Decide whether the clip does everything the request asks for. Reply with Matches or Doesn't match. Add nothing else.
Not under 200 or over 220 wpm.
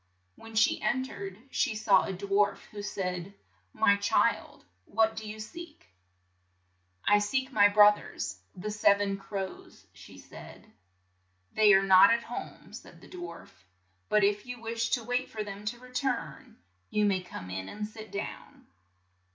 Doesn't match